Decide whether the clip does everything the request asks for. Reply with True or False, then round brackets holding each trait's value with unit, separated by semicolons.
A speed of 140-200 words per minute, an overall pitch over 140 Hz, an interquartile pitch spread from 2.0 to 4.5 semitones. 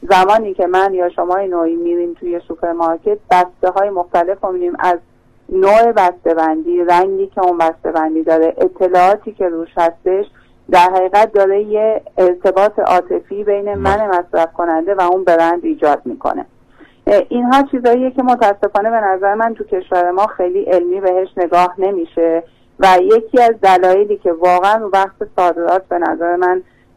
True (155 wpm; 185 Hz; 2.8 semitones)